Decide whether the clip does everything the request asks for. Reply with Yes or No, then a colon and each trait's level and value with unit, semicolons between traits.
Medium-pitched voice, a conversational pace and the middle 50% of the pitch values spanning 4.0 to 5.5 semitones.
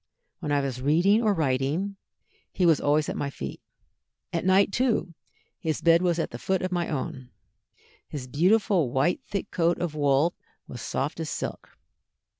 Yes: medium, 165 Hz; average, 165 wpm; average, 4.7 semitones